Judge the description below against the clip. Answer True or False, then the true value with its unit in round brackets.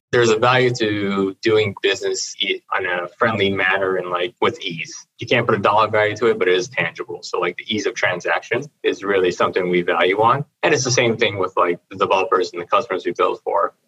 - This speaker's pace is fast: True (230 wpm)